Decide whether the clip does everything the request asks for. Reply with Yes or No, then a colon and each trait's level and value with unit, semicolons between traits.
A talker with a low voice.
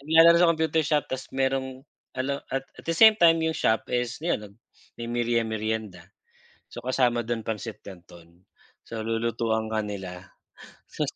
Yes: low, 120 Hz